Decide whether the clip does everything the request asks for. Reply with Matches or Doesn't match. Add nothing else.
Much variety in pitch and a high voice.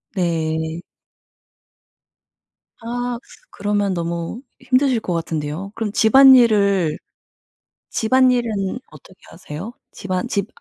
Matches